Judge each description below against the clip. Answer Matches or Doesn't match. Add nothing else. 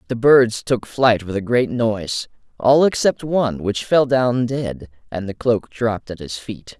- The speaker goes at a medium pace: Matches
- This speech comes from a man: Matches